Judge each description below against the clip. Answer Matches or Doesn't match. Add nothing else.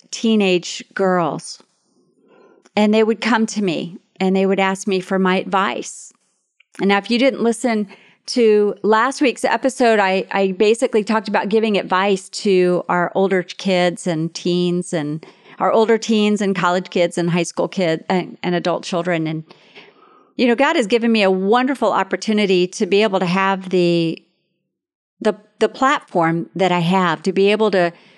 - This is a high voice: Matches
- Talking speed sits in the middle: Matches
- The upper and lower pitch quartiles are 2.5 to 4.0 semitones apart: Matches